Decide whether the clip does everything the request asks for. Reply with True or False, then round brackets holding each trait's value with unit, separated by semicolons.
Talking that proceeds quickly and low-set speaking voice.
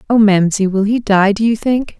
False (240 wpm; 210 Hz)